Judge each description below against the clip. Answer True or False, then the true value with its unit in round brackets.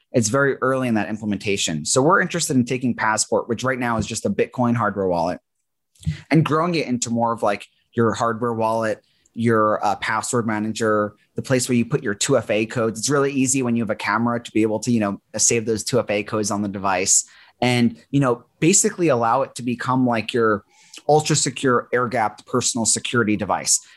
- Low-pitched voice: True (115 Hz)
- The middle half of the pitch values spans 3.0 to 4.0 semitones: True (3.3 semitones)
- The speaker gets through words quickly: True (210 wpm)